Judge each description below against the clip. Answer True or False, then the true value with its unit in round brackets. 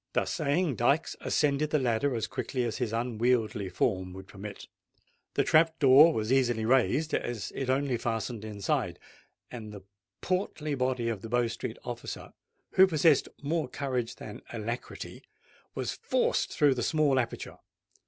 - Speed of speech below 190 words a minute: True (155 wpm)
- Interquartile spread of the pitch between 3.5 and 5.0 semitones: True (4.1 semitones)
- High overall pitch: False (125 Hz)